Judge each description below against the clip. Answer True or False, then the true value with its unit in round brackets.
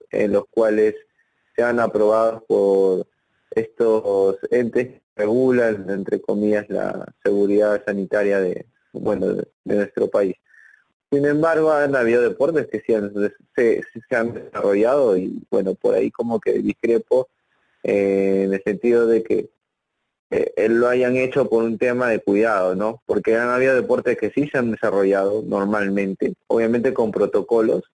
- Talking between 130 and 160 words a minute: True (150 wpm)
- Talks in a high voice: False (120 Hz)